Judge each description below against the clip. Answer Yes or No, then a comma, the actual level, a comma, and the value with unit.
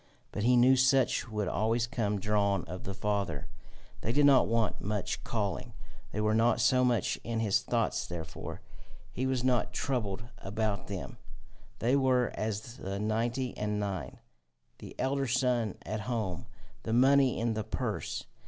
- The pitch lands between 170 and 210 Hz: No, low, 110 Hz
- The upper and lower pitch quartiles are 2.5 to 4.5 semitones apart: Yes, average, 3.5 semitones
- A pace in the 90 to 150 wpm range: No, average, 160 wpm